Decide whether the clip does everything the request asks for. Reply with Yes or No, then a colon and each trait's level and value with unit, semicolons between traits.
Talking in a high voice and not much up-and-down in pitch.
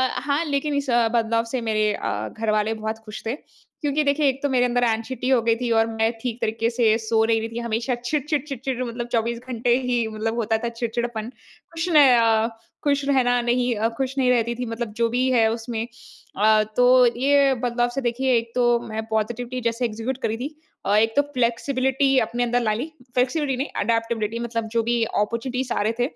Yes: high, 240 Hz; narrow, 2.3 semitones